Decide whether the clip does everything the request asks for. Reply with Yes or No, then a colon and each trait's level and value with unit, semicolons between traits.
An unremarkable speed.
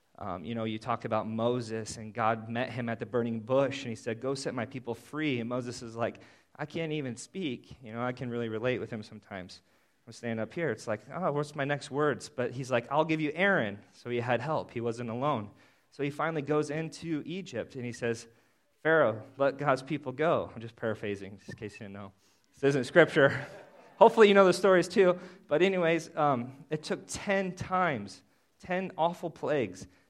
No: fast, 215 wpm